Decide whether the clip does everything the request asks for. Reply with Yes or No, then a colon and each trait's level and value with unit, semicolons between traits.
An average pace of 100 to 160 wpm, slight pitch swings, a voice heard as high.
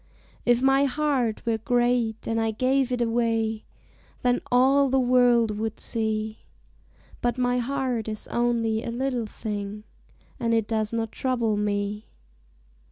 Yes: average, 140 wpm; narrow, 2.1 semitones; high, 235 Hz